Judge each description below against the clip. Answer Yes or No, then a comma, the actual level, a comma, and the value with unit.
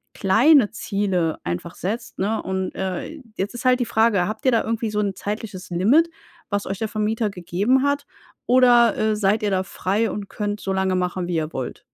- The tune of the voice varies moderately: Yes, average, 3.3 semitones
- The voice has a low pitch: No, high, 205 Hz